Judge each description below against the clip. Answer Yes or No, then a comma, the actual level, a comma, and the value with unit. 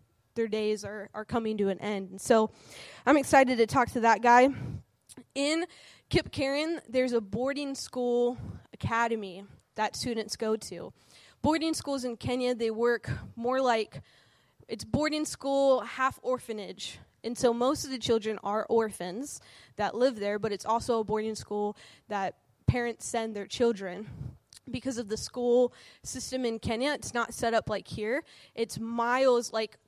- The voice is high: Yes, high, 235 Hz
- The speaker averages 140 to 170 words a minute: Yes, average, 160 wpm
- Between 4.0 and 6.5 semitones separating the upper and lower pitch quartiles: No, average, 2.9 semitones